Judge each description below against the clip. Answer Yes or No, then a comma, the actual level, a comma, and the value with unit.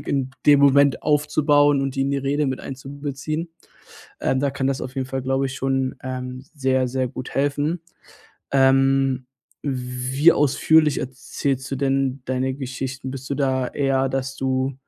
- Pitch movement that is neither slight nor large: No, narrow, 1.3 semitones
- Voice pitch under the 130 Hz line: No, low, 135 Hz